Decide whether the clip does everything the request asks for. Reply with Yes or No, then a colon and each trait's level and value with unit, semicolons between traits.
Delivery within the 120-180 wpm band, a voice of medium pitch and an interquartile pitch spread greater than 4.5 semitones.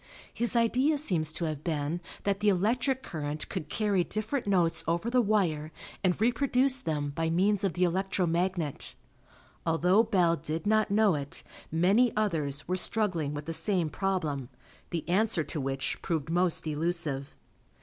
Yes: average, 160 wpm; medium, 175 Hz; average, 5.0 semitones